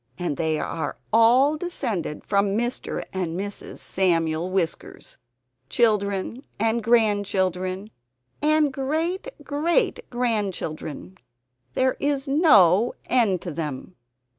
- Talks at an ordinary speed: No, slow, 100 wpm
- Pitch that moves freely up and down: Yes, wide, 6.1 semitones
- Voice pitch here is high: Yes, high, 205 Hz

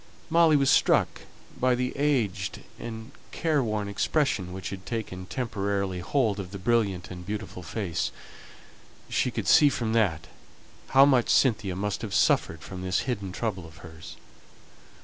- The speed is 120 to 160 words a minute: Yes, average, 150 wpm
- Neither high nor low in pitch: No, low, 105 Hz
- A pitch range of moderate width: Yes, average, 4.9 semitones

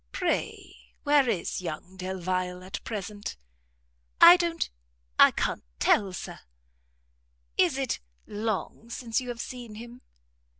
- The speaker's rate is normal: No, slow, 120 wpm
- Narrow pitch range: No, average, 4.7 semitones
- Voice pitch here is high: Yes, high, 210 Hz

